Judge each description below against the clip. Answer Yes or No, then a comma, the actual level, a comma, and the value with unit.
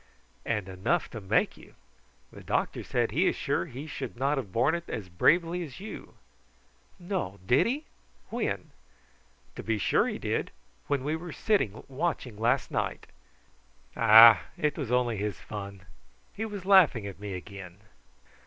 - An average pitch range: No, wide, 8.3 semitones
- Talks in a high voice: No, low, 120 Hz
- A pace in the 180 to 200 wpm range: No, average, 160 wpm